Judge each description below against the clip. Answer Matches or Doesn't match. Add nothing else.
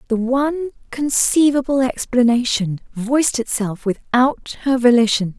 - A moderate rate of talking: Doesn't match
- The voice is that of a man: Doesn't match